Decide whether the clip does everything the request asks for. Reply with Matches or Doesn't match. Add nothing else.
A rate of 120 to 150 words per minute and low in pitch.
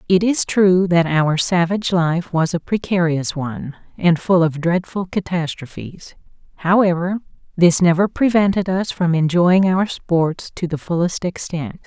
Doesn't match